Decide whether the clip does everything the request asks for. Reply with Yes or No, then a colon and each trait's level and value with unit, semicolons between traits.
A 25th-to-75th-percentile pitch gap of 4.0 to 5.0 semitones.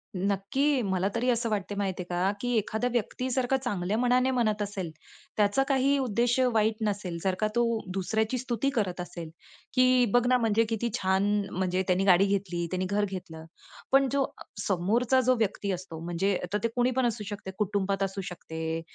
Yes: average, 4.5 semitones